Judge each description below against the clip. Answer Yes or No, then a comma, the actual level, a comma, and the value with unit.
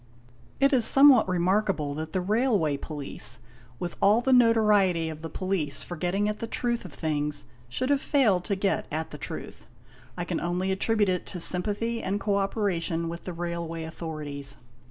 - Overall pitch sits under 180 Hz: No, medium, 185 Hz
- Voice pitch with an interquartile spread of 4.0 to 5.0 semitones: Yes, average, 4.7 semitones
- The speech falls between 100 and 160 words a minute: No, average, 175 wpm